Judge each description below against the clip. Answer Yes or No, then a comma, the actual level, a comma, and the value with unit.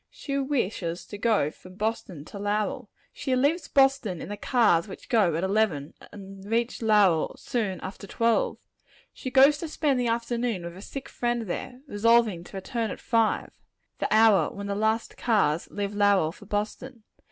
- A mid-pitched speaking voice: No, high, 215 Hz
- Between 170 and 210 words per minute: Yes, average, 175 wpm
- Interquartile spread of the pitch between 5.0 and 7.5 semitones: No, average, 3.7 semitones